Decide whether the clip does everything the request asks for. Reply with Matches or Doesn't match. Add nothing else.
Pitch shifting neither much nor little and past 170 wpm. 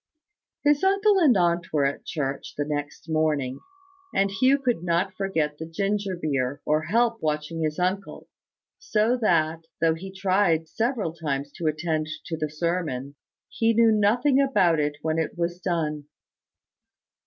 Doesn't match